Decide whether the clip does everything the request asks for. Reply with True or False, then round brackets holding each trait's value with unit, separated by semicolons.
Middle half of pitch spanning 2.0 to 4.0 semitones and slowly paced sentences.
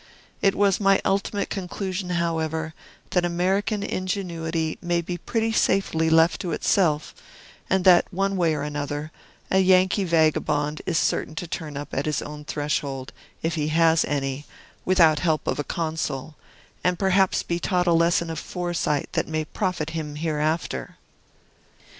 False (3.1 semitones; 155 wpm)